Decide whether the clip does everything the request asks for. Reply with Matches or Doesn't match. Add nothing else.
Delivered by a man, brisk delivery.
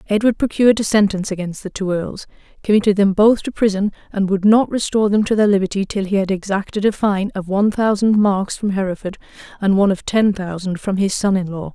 Doesn't match